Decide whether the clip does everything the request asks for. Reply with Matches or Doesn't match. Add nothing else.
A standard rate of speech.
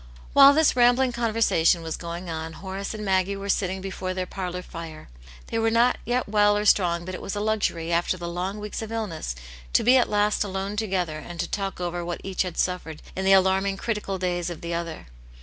Doesn't match